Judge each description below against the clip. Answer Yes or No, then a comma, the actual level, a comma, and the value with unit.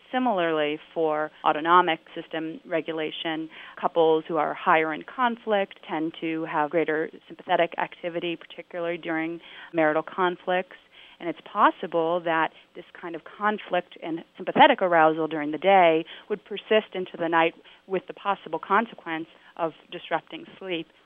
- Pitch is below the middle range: No, medium, 170 Hz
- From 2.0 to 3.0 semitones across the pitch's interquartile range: Yes, narrow, 2.6 semitones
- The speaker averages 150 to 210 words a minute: No, slow, 135 wpm